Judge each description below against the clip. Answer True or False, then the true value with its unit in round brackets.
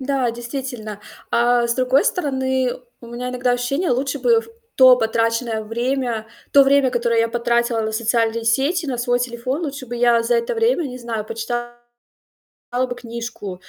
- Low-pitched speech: False (245 Hz)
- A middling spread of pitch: False (2.3 semitones)